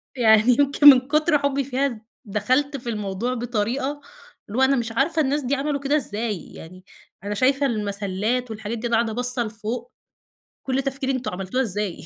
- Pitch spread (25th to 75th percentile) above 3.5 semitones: Yes, average, 4.3 semitones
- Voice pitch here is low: No, high, 245 Hz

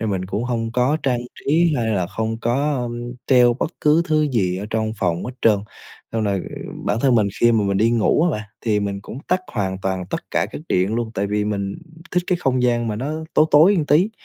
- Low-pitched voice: Yes, low, 115 Hz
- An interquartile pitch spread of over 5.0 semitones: No, average, 4.7 semitones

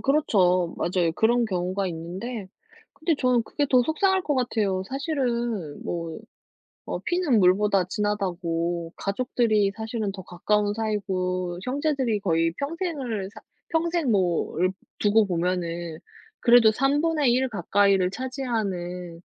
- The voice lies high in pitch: Yes, high, 210 Hz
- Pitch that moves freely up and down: Yes, wide, 5.8 semitones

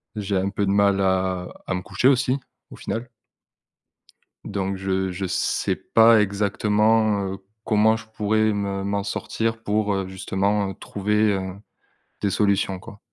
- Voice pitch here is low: Yes, low, 100 Hz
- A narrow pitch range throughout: Yes, narrow, 1.9 semitones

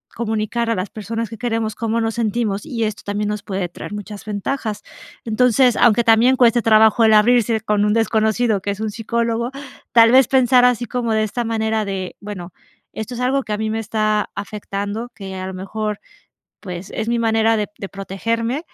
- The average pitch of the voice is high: Yes, high, 220 Hz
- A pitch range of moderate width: No, narrow, 2.0 semitones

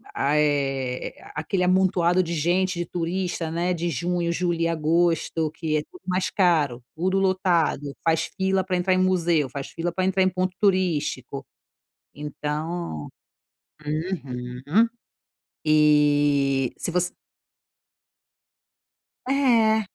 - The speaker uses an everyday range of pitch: Yes, average, 3.8 semitones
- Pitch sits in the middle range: Yes, medium, 170 Hz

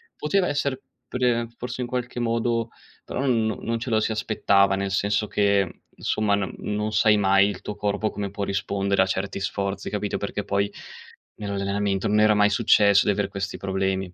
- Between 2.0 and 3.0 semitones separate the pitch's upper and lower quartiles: Yes, narrow, 2.5 semitones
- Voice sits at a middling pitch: No, low, 105 Hz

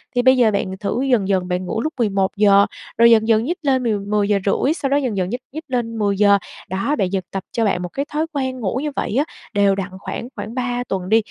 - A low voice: No, high, 220 Hz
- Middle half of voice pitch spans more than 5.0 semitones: No, average, 4.5 semitones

